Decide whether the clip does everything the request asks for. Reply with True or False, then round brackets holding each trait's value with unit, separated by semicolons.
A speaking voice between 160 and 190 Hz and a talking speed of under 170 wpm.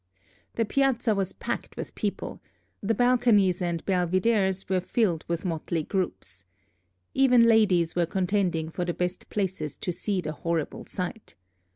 True (185 Hz; 145 wpm)